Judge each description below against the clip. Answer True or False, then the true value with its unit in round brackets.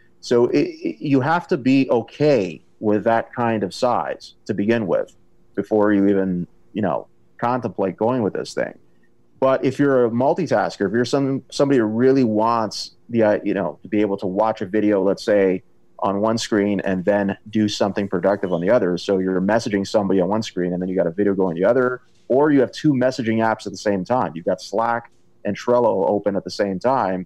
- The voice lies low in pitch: True (105 Hz)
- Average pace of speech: False (215 wpm)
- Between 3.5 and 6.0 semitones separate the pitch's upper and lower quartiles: True (3.8 semitones)